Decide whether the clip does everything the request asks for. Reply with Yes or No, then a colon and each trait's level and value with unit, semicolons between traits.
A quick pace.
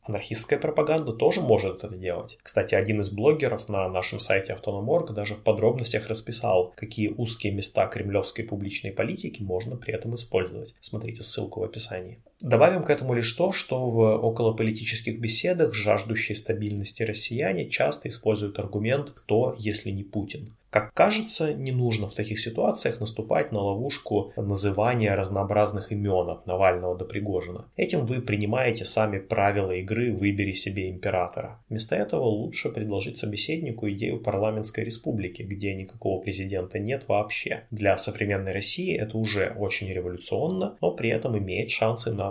No: average, 145 wpm